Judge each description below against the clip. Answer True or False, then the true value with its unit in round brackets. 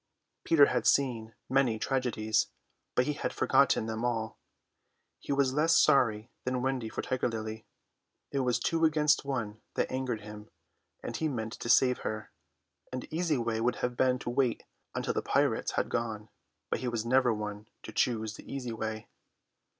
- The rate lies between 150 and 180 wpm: True (175 wpm)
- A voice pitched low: True (125 Hz)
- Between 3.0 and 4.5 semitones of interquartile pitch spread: True (3.3 semitones)